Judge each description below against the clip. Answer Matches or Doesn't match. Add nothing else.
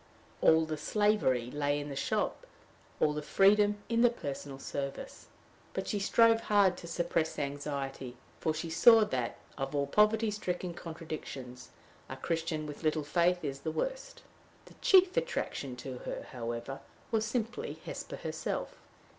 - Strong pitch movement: Matches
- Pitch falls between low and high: Matches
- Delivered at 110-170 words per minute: Matches